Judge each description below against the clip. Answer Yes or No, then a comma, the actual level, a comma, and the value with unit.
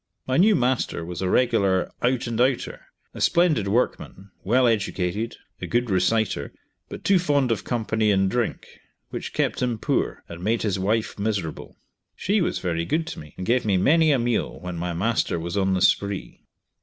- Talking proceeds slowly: No, average, 185 wpm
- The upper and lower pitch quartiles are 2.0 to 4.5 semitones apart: No, average, 4.9 semitones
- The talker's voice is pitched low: Yes, low, 110 Hz